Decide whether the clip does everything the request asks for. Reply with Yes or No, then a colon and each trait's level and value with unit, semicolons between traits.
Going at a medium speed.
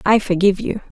Yes: average, 180 wpm